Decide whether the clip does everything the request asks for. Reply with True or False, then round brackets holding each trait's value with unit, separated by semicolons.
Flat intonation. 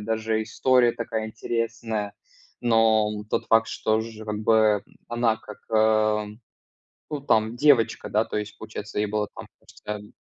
True (1.2 semitones)